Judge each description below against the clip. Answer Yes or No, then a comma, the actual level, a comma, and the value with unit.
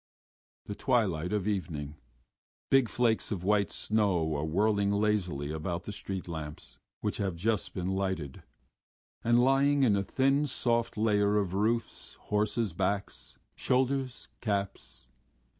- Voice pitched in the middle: No, low, 100 Hz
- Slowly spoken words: Yes, slow, 130 wpm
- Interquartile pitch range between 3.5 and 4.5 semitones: Yes, average, 4.2 semitones